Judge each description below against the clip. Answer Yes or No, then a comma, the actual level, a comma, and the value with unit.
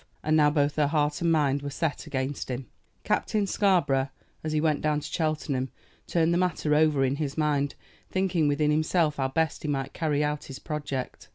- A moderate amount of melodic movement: No, narrow, 1.9 semitones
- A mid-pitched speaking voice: Yes, medium, 150 Hz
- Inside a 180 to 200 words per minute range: Yes, average, 195 wpm